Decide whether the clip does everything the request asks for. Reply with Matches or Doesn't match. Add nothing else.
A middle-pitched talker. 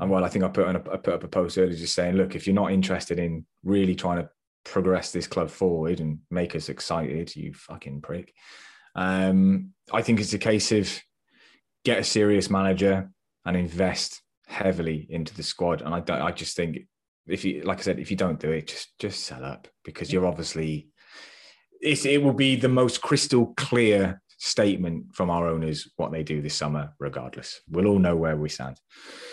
Doesn't match